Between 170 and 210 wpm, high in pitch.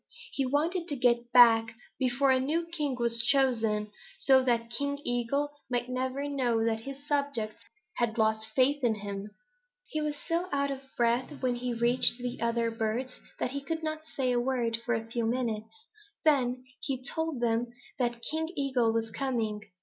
Yes: average, 175 wpm; very high, 250 Hz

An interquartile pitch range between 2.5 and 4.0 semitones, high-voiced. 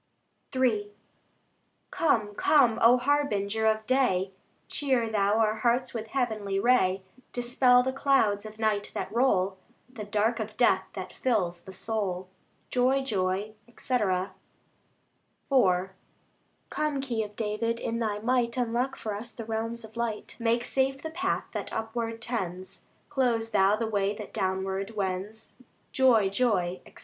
Yes: average, 3.5 semitones; high, 220 Hz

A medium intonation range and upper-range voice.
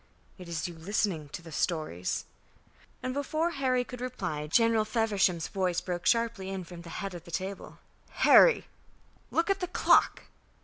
No: wide, 6.4 semitones; high, 195 Hz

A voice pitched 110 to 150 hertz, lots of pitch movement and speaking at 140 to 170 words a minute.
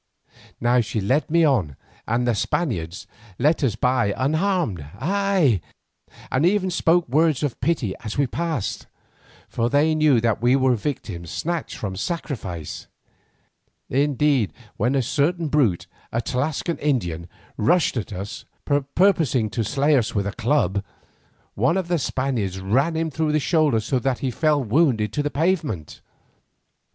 Yes: low, 135 Hz; wide, 6.1 semitones; average, 150 wpm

